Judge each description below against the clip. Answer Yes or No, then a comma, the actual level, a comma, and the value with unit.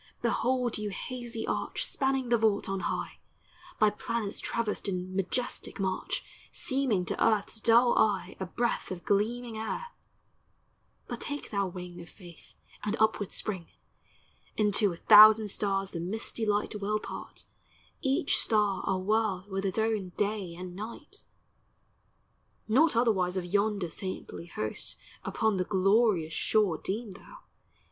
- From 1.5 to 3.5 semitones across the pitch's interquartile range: Yes, average, 3.2 semitones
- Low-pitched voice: No, high, 210 Hz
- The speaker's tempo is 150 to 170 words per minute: No, average, 140 wpm